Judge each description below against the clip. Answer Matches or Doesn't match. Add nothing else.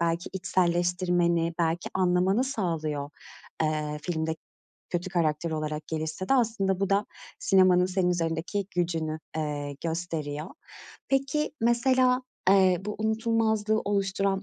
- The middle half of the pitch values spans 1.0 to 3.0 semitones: Doesn't match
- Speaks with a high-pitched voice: Doesn't match